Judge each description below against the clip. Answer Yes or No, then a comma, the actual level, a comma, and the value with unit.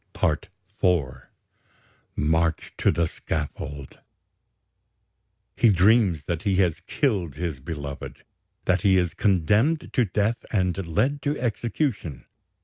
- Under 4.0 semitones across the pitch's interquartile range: No, average, 5.0 semitones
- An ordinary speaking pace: No, slow, 115 wpm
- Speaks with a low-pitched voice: Yes, very low, 90 Hz